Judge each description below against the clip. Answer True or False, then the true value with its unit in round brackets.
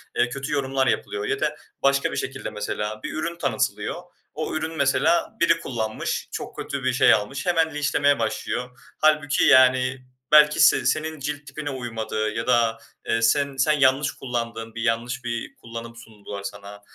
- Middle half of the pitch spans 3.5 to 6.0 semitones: True (4.2 semitones)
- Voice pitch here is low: True (130 Hz)